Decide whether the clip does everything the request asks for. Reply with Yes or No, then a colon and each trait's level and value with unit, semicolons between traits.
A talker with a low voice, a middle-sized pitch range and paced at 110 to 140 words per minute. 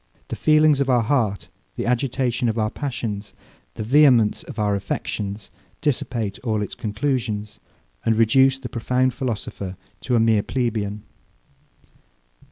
Yes: low, 115 Hz; average, 3.6 semitones; slow, 135 wpm